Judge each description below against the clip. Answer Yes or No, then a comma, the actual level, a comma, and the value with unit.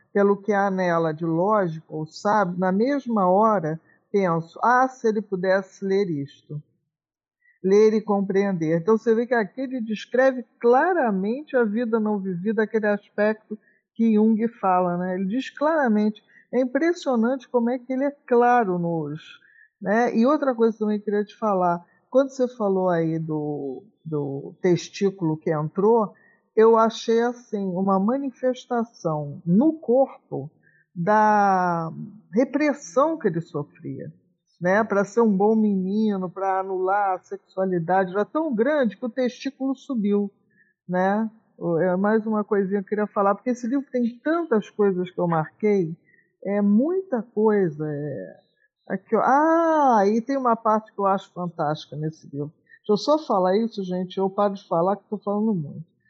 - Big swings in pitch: No, average, 4.4 semitones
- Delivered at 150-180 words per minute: Yes, average, 155 wpm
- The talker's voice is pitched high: Yes, high, 205 Hz